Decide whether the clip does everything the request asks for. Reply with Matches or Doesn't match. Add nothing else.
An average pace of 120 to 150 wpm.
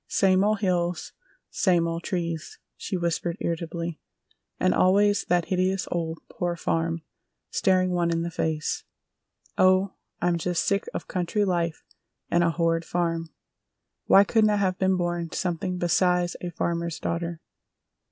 Matches